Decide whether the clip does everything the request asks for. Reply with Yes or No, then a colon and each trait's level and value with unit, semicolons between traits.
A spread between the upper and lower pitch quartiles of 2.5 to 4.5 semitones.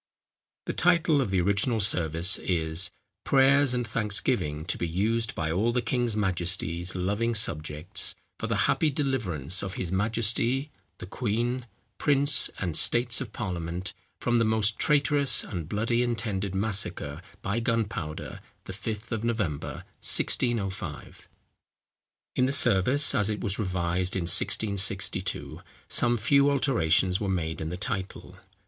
No: average, 4.9 semitones